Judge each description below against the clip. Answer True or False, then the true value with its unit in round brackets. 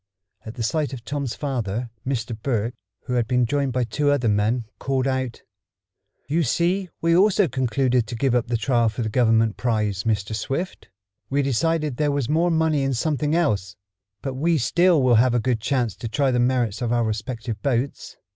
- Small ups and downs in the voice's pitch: False (3.9 semitones)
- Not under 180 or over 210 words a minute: True (195 wpm)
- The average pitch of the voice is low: True (125 Hz)